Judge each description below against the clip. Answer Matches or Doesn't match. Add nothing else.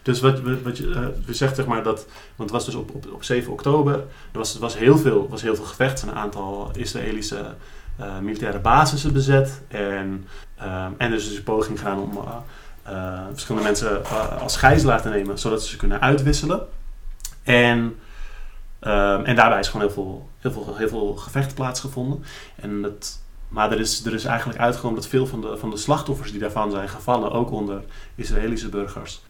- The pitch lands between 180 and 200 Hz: Doesn't match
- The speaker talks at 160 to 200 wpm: Matches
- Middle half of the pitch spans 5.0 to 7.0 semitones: Doesn't match